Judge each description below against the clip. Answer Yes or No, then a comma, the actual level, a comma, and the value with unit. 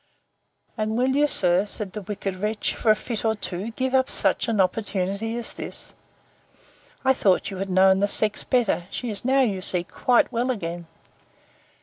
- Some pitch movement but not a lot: Yes, average, 3.9 semitones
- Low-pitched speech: No, high, 210 Hz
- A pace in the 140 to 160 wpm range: No, average, 180 wpm